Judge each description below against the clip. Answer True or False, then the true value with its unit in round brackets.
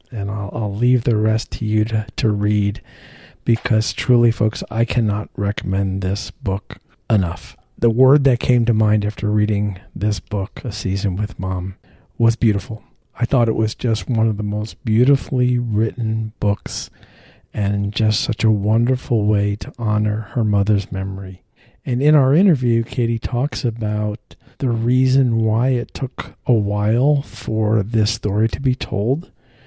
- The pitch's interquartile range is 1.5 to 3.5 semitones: True (2.7 semitones)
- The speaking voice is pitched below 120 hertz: True (110 Hz)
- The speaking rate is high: False (160 wpm)